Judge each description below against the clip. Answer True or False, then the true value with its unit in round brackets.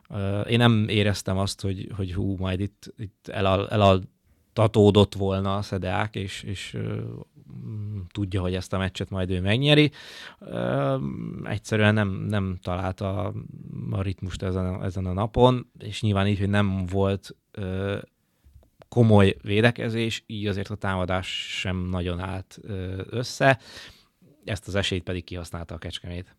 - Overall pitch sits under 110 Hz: True (100 Hz)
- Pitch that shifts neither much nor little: False (2.2 semitones)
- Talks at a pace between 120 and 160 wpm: True (130 wpm)